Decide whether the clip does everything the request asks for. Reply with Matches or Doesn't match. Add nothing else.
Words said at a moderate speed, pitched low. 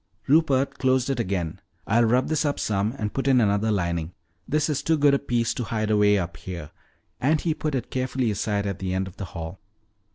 Doesn't match